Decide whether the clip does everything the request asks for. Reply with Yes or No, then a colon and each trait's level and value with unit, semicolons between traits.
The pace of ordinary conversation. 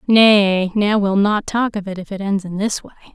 No: fast, 250 wpm